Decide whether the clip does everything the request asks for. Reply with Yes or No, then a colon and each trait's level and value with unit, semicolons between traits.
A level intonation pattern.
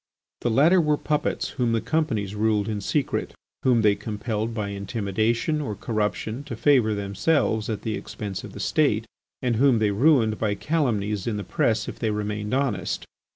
No: average, 3.6 semitones